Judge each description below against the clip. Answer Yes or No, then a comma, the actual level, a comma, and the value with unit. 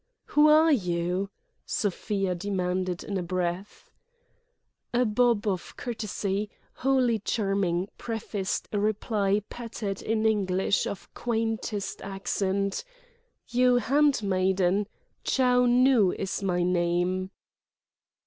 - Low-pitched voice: No, high, 200 Hz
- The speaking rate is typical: No, slow, 95 wpm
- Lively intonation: No, average, 3.7 semitones